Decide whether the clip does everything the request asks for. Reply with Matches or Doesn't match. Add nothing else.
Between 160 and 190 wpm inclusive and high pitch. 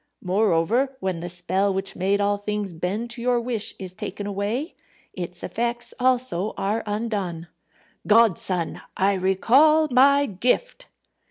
Doesn't match